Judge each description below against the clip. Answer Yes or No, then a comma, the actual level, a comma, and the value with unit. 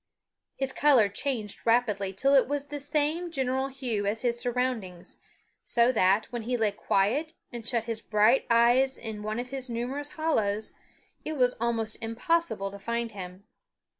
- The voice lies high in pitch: Yes, high, 235 Hz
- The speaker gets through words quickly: No, average, 165 wpm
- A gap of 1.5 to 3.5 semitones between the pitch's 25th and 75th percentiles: No, average, 3.9 semitones